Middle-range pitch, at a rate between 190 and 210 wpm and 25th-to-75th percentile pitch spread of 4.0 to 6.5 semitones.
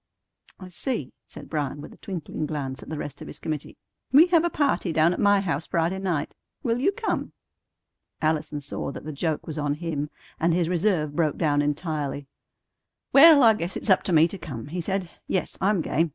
Yes: medium, 165 Hz; fast, 205 wpm; average, 4.5 semitones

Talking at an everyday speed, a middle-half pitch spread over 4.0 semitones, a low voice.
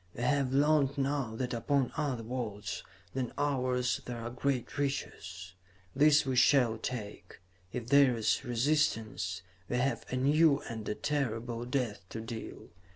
No: average, 150 wpm; average, 3.6 semitones; low, 125 Hz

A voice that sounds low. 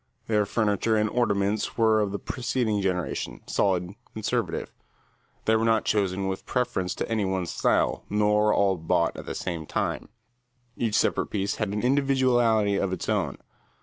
Yes: low, 105 Hz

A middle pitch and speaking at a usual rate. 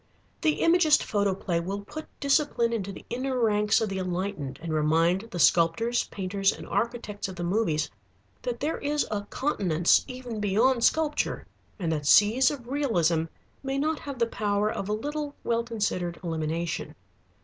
No: high, 210 Hz; average, 160 wpm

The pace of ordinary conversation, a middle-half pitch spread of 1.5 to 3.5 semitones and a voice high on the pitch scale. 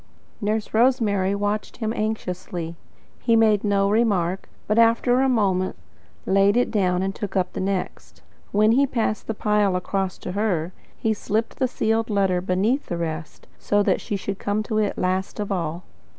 Yes: average, 180 wpm; average, 2.8 semitones; high, 205 Hz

